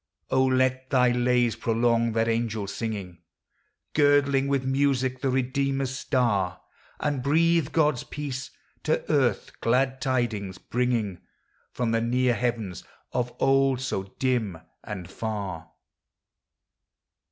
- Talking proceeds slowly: Yes, slow, 115 wpm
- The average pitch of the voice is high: No, low, 125 Hz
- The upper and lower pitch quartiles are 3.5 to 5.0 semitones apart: No, average, 3.0 semitones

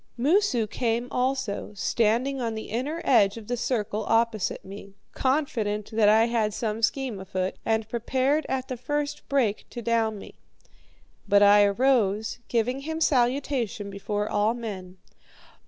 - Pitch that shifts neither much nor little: Yes, average, 3.8 semitones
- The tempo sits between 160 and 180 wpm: No, average, 145 wpm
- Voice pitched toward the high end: Yes, high, 230 Hz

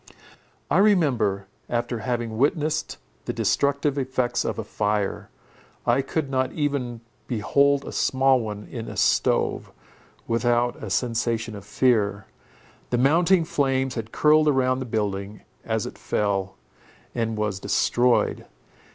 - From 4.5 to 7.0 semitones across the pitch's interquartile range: No, average, 3.9 semitones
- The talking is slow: Yes, slow, 130 wpm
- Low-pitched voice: Yes, low, 120 Hz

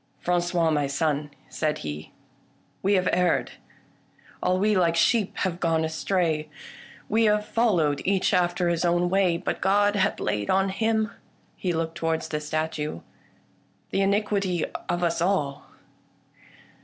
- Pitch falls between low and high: Yes, medium, 175 Hz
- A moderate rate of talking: Yes, average, 165 wpm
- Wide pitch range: No, average, 3.5 semitones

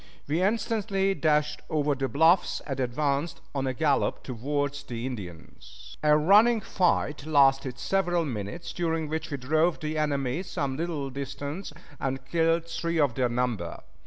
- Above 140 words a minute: Yes, average, 150 wpm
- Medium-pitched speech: Yes, medium, 150 Hz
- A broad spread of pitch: No, average, 3.7 semitones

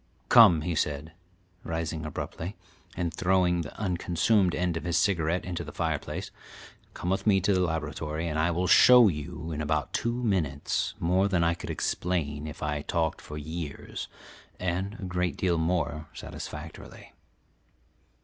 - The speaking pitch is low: Yes, very low, 85 Hz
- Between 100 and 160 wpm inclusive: Yes, average, 155 wpm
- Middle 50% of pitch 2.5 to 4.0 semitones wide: Yes, average, 2.8 semitones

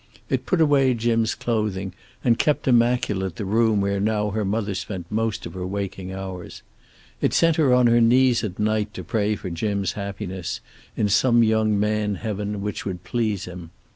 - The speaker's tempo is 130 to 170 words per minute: No, average, 180 wpm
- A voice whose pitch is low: Yes, low, 105 Hz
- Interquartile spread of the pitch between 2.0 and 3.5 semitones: Yes, average, 3.0 semitones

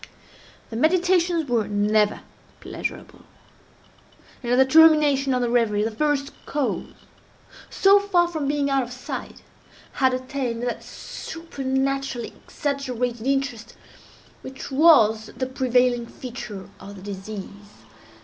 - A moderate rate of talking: No, slow, 120 wpm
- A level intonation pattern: No, average, 3.7 semitones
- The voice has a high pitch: Yes, very high, 260 Hz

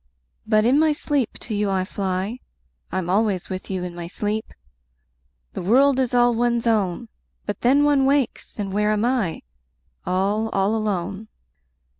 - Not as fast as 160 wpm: No, average, 165 wpm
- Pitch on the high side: Yes, high, 215 Hz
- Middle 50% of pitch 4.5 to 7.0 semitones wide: No, average, 4.1 semitones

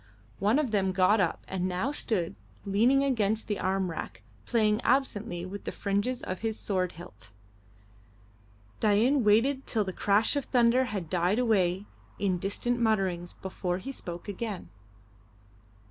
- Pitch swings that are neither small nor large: Yes, average, 4.1 semitones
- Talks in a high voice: Yes, high, 205 Hz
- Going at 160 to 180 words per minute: No, average, 145 wpm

